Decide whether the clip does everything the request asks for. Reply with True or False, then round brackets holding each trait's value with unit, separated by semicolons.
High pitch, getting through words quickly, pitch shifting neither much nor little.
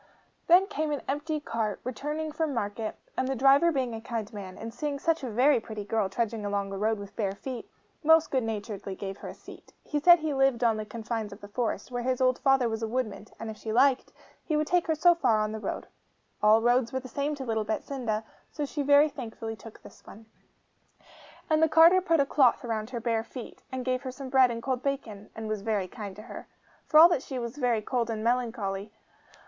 True (240 Hz; 230 wpm; 4.4 semitones)